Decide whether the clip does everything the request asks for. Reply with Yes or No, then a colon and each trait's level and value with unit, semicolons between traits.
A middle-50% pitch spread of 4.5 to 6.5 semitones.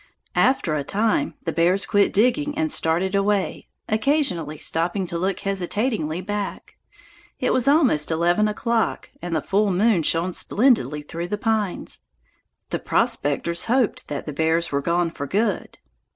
Yes: average, 4.9 semitones